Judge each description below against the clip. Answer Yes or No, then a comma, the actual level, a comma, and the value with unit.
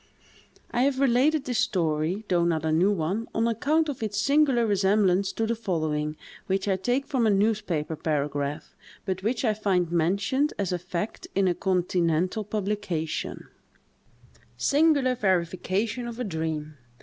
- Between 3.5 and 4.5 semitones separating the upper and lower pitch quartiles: No, average, 5.3 semitones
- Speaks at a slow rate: No, average, 150 wpm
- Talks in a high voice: Yes, high, 195 Hz